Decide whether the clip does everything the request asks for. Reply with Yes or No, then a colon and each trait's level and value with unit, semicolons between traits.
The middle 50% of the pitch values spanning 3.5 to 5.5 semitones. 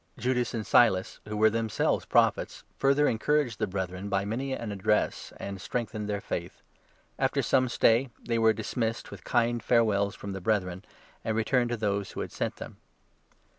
No: average, 3.0 semitones